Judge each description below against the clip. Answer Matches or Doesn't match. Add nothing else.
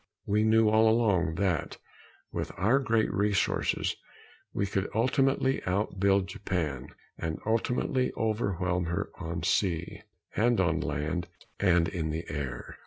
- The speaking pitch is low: Matches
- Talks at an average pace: Doesn't match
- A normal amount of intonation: Matches